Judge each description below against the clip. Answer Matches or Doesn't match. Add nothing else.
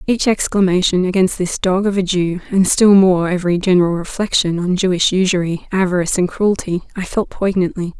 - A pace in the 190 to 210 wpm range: Doesn't match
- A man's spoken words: Doesn't match